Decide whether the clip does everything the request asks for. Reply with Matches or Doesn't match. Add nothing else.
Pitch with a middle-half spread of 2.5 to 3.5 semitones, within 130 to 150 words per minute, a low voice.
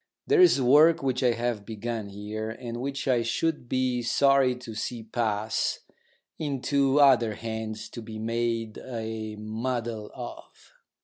Matches